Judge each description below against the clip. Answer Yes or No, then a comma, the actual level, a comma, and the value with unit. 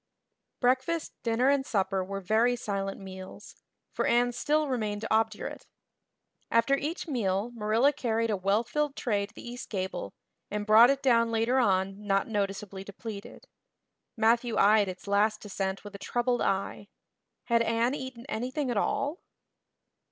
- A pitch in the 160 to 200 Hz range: No, high, 225 Hz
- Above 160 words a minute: No, average, 150 wpm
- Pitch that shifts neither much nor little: Yes, average, 3.5 semitones